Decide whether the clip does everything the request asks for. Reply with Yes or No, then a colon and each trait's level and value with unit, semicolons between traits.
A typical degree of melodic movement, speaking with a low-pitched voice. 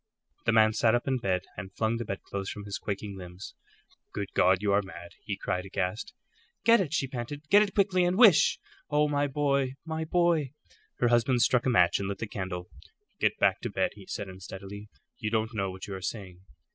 No: wide, 6.2 semitones; low, 110 Hz